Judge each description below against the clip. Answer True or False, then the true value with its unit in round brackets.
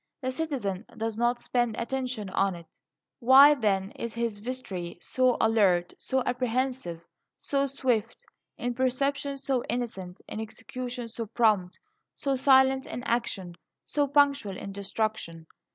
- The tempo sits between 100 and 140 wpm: True (135 wpm)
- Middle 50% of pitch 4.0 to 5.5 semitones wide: True (4.3 semitones)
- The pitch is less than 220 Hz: False (240 Hz)